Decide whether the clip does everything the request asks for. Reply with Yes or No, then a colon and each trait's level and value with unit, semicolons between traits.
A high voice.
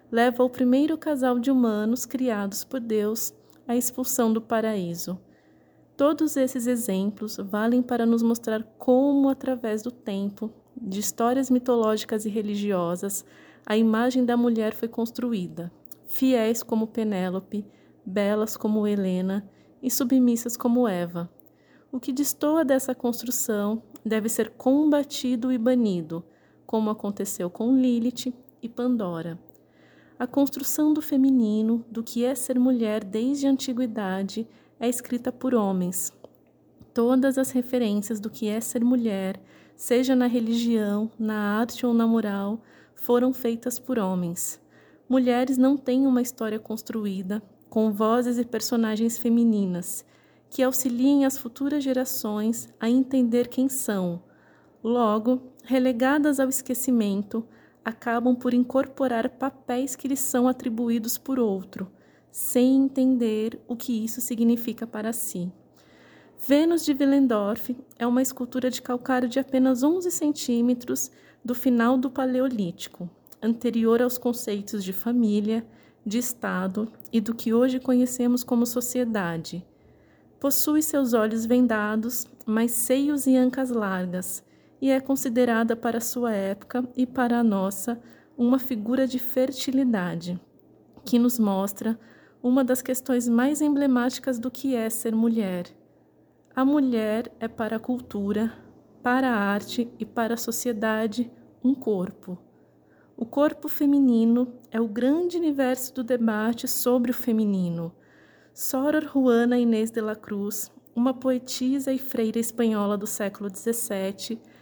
Yes: high, 240 Hz